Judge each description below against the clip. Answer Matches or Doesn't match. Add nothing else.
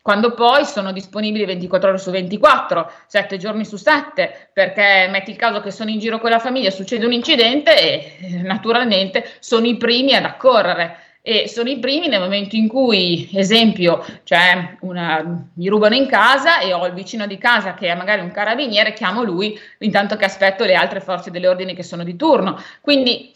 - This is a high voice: Matches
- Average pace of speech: Doesn't match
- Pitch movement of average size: Matches